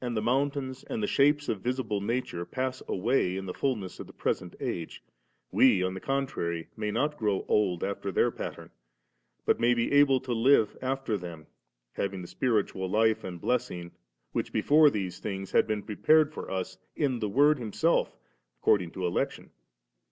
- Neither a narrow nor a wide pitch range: No, wide, 5.9 semitones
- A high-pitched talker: No, low, 110 Hz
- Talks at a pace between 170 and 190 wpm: Yes, average, 175 wpm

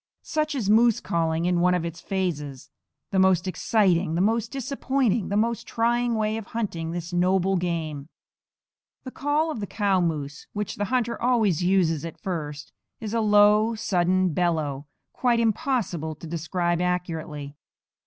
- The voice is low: No, medium, 185 Hz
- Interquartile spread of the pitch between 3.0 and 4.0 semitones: No, average, 5.1 semitones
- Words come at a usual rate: Yes, average, 155 wpm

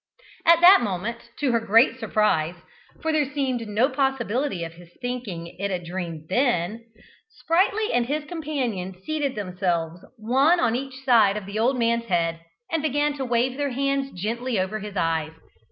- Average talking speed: Yes, average, 170 wpm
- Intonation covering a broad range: Yes, wide, 6.4 semitones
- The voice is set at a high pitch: Yes, high, 235 Hz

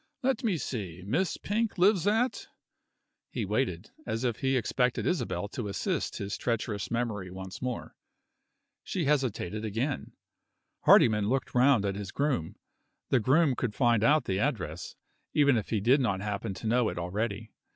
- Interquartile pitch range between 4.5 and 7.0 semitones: Yes, wide, 5.6 semitones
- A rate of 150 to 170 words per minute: Yes, average, 160 wpm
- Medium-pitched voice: No, low, 115 Hz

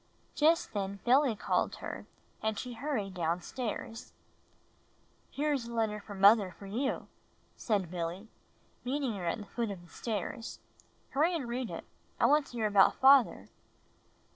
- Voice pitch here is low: No, high, 225 Hz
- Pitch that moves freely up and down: No, average, 4.8 semitones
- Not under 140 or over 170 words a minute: Yes, average, 160 wpm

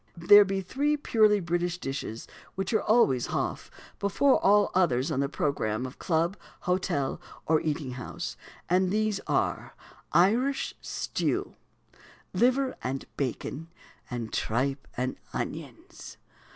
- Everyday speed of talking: No, slow, 125 wpm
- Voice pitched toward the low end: No, medium, 175 Hz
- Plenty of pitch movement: Yes, wide, 7.2 semitones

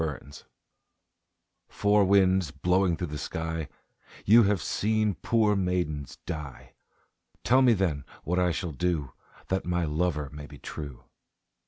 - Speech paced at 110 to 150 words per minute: Yes, average, 140 wpm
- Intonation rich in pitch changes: No, average, 4.5 semitones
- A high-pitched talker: No, very low, 90 Hz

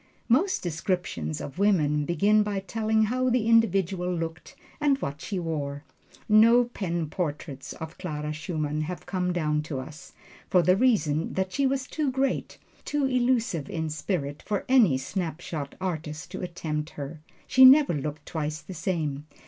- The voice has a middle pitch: Yes, medium, 175 Hz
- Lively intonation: Yes, wide, 6.2 semitones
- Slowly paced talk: No, average, 155 wpm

